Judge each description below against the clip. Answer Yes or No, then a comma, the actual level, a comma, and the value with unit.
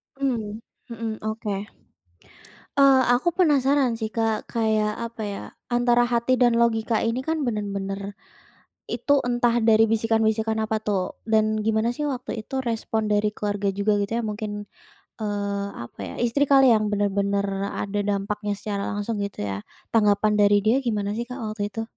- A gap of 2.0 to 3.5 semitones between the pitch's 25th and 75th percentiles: Yes, narrow, 2.5 semitones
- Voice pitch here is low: No, high, 220 Hz